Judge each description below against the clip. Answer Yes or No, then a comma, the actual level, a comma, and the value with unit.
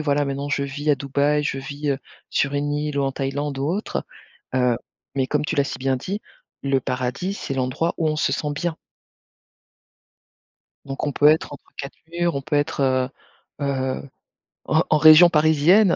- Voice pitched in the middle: Yes, medium, 145 Hz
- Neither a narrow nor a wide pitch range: No, narrow, 2.1 semitones